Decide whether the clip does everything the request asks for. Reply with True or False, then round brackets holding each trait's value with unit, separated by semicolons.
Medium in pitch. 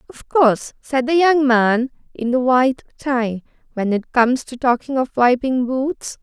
False (255 Hz)